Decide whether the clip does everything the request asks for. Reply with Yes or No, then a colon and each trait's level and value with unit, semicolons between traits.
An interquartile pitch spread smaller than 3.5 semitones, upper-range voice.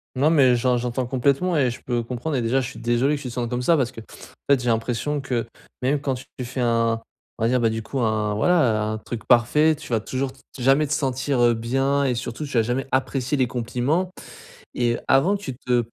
No: narrow, 2.6 semitones; low, 125 Hz